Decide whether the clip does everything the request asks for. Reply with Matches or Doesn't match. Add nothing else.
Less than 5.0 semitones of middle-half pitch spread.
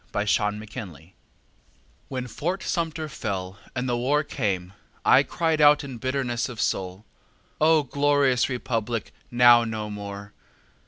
Doesn't match